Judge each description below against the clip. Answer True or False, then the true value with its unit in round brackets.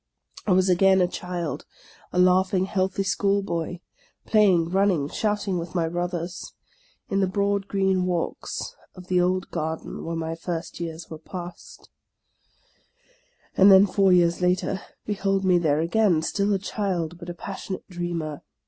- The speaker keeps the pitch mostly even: True (2.2 semitones)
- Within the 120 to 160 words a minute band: True (155 wpm)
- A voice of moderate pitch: True (180 Hz)